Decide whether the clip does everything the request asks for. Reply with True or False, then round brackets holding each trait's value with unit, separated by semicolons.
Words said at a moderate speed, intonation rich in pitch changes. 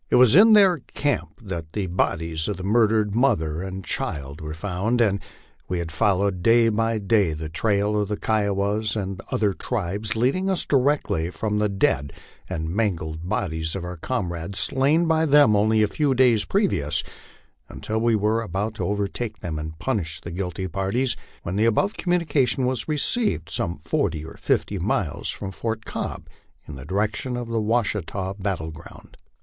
False (170 wpm; 5.0 semitones)